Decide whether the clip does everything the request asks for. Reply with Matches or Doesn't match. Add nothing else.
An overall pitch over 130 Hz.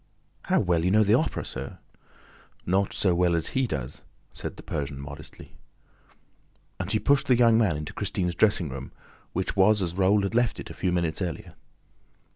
Doesn't match